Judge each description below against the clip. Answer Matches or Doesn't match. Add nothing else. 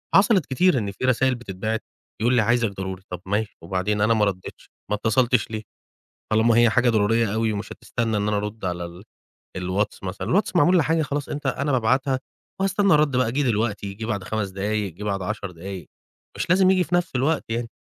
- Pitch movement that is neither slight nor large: Matches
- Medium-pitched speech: Doesn't match